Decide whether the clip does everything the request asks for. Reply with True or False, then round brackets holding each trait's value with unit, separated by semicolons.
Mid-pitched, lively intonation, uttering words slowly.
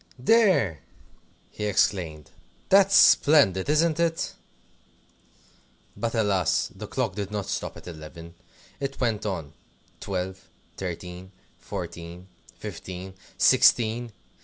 False (100 Hz; 5.7 semitones; 100 wpm)